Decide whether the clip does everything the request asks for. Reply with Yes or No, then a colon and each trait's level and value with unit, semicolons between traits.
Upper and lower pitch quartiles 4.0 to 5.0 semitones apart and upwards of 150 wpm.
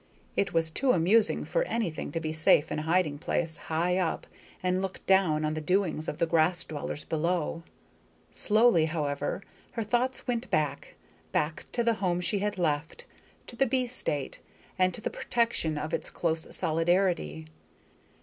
Yes: average, 4.5 semitones; average, 170 wpm